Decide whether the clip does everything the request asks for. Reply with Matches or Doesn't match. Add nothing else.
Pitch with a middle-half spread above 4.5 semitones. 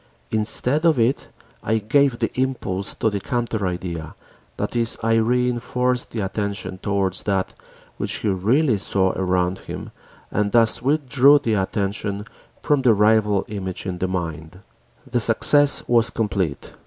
Doesn't match